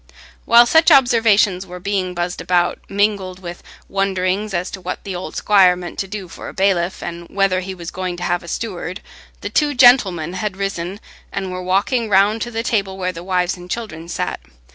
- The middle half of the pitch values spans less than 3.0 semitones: Yes, narrow, 2.5 semitones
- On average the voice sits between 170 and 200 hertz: Yes, high, 190 Hz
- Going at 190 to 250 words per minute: Yes, average, 200 wpm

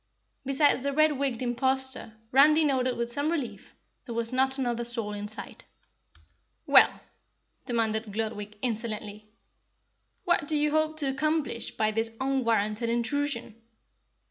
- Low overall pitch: No, high, 245 Hz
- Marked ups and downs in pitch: No, average, 3.8 semitones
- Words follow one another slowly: Yes, slow, 130 wpm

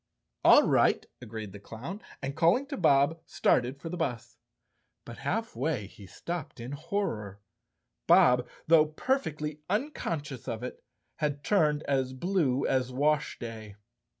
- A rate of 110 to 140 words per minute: Yes, slow, 135 wpm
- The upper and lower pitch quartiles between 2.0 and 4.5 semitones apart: No, average, 4.9 semitones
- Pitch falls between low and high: Yes, medium, 145 Hz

